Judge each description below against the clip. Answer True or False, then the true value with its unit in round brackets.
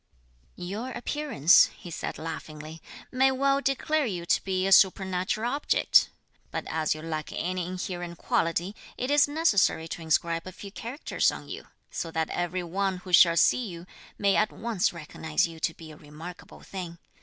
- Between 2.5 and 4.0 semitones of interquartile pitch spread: False (4.6 semitones)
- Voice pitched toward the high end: False (180 Hz)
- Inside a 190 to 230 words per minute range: False (170 wpm)